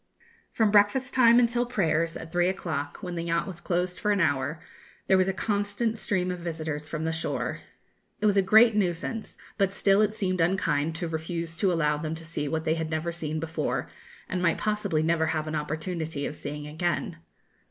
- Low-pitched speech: No, medium, 170 Hz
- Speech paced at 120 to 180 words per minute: No, average, 200 wpm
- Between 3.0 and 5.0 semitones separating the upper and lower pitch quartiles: Yes, average, 3.8 semitones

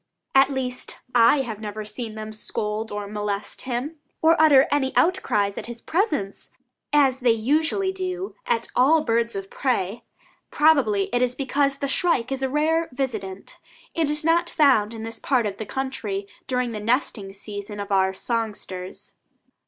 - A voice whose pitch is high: Yes, high, 245 Hz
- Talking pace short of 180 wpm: Yes, average, 160 wpm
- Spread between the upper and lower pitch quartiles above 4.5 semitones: Yes, average, 5.3 semitones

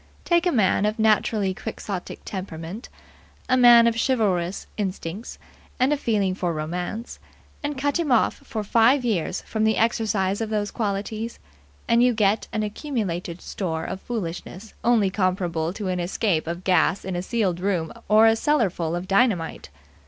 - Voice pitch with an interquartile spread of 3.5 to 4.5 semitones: Yes, average, 4.0 semitones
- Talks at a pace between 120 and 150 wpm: No, average, 160 wpm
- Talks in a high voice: Yes, high, 205 Hz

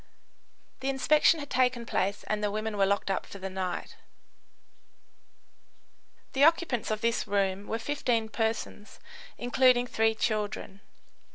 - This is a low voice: No, high, 220 Hz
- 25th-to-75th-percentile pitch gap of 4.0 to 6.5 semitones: No, average, 3.6 semitones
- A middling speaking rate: No, slow, 130 wpm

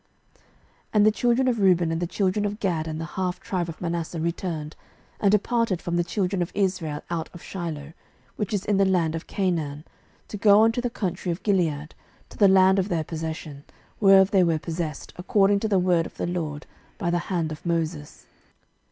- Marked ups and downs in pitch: No, average, 3.3 semitones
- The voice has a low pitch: No, medium, 180 Hz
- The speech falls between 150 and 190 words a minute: No, fast, 205 wpm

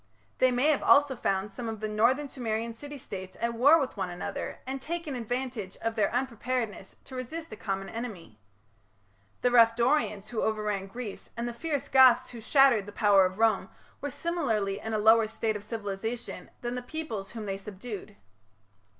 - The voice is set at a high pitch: Yes, high, 230 Hz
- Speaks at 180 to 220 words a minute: Yes, average, 185 wpm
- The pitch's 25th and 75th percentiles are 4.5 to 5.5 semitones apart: No, average, 3.7 semitones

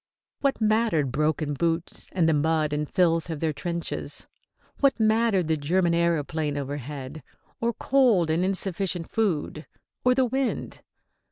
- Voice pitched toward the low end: No, medium, 170 Hz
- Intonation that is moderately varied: No, wide, 5.8 semitones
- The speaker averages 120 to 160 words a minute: Yes, average, 140 wpm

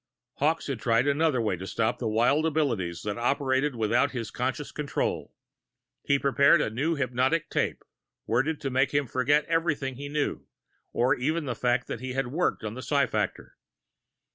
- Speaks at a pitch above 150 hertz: No, low, 130 Hz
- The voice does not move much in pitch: No, average, 3.4 semitones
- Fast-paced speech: No, average, 175 wpm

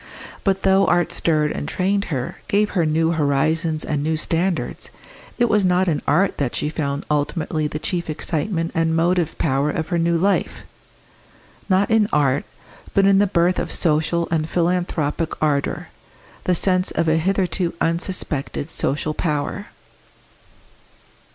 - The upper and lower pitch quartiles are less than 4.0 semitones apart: Yes, average, 3.2 semitones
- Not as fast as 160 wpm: Yes, average, 150 wpm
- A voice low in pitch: No, medium, 165 Hz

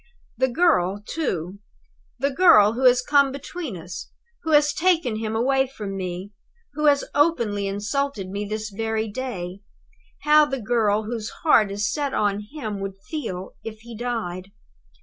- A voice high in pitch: Yes, high, 225 Hz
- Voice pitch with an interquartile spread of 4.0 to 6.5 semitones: Yes, wide, 5.6 semitones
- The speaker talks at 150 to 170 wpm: Yes, average, 160 wpm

